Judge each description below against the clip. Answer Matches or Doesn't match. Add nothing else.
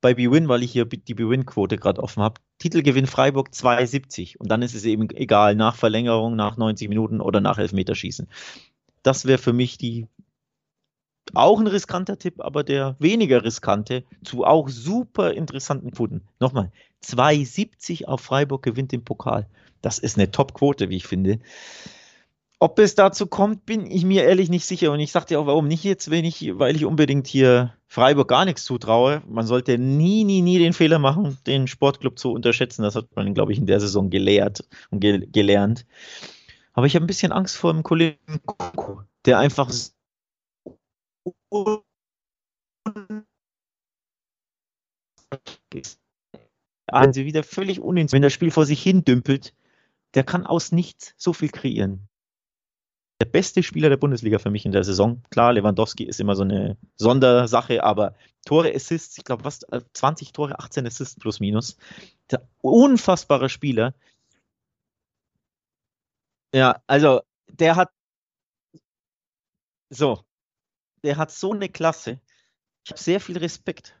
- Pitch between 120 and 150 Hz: Matches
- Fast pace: Doesn't match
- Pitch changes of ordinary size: Doesn't match